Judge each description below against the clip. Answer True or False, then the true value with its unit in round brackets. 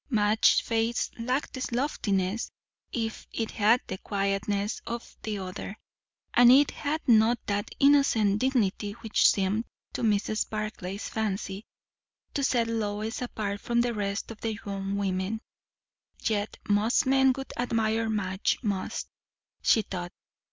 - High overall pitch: True (215 Hz)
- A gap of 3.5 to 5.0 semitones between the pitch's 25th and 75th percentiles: False (2.7 semitones)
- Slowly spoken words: True (130 wpm)